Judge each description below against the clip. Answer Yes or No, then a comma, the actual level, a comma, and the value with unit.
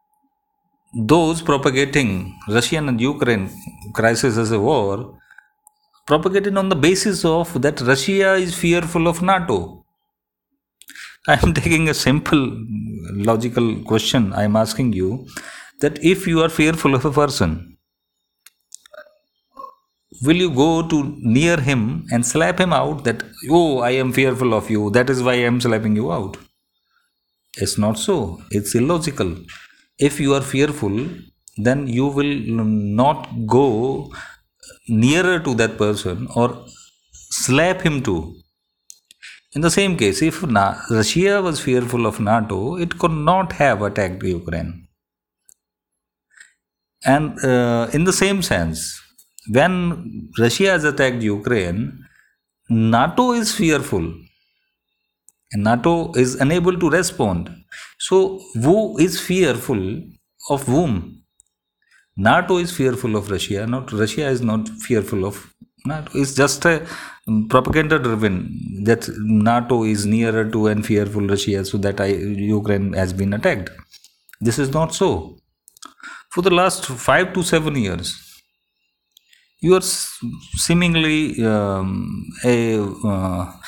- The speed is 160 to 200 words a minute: No, average, 125 wpm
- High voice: No, low, 125 Hz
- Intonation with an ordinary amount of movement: No, wide, 7.7 semitones